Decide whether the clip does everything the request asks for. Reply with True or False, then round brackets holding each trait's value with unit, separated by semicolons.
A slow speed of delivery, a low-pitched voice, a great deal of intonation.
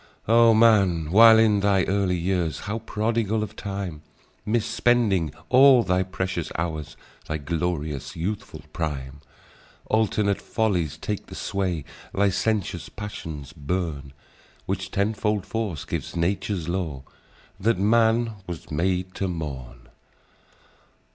False (115 wpm; 95 Hz; 4.8 semitones)